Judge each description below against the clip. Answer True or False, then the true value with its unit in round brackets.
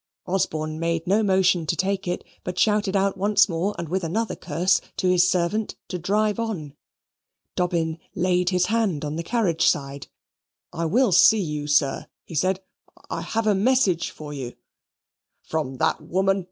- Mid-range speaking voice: True (180 Hz)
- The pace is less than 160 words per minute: False (165 wpm)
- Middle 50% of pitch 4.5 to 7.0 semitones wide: False (3.6 semitones)